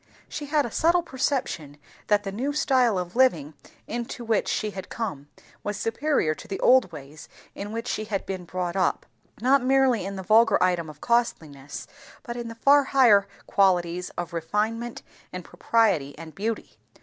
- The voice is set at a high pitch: Yes, high, 210 Hz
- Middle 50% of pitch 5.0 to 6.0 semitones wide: Yes, average, 5.3 semitones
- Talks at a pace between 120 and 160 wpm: No, average, 175 wpm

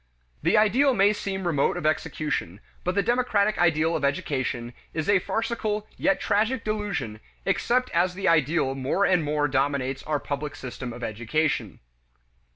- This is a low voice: No, medium, 165 Hz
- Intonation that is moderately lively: No, wide, 6.8 semitones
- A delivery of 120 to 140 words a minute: No, average, 155 wpm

